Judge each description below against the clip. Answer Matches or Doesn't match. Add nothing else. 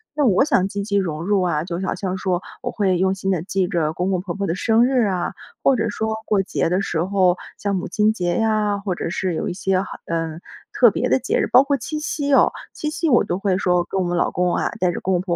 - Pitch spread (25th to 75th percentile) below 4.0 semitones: Matches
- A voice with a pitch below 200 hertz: Matches